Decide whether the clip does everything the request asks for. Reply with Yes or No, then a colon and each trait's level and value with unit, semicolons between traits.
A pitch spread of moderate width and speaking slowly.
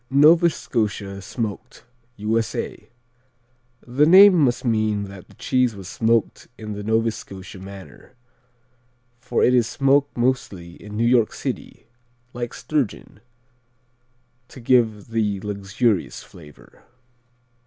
Yes: average, 3.7 semitones; slow, 115 wpm